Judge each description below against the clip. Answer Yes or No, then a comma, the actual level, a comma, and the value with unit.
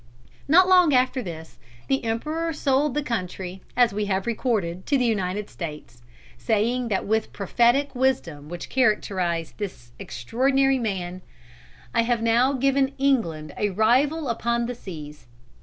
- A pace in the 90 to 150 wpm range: Yes, average, 140 wpm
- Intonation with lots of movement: Yes, wide, 6.4 semitones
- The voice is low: No, high, 230 Hz